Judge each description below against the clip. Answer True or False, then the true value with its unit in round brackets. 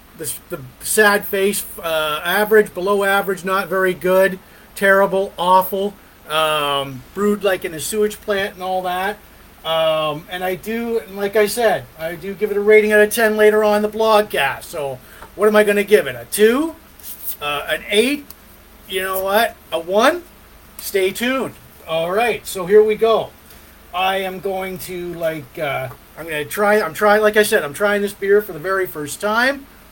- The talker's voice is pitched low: False (195 Hz)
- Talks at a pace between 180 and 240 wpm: True (190 wpm)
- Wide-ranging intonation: False (2.8 semitones)